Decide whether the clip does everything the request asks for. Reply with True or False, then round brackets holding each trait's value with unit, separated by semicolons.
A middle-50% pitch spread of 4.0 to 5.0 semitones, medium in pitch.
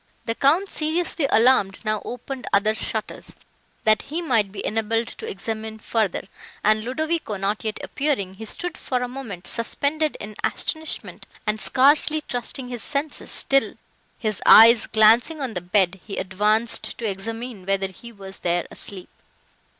False (4.7 semitones; 225 Hz)